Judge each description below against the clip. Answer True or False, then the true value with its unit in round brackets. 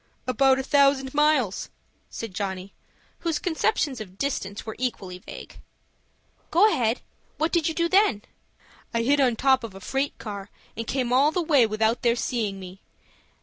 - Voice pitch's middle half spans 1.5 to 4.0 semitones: False (5.2 semitones)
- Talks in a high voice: True (255 Hz)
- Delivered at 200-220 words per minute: False (165 wpm)